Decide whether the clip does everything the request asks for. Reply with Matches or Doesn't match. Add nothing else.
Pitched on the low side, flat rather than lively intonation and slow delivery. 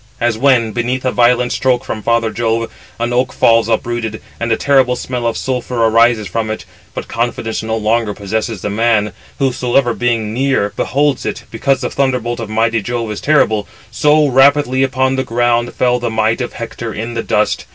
Doesn't match